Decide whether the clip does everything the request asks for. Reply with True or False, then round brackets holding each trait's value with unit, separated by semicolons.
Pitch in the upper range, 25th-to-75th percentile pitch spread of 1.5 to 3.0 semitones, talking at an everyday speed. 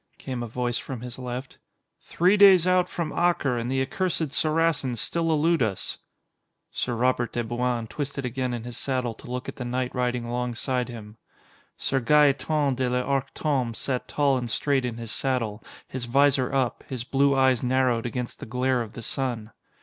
False (125 Hz; 2.5 semitones; 180 wpm)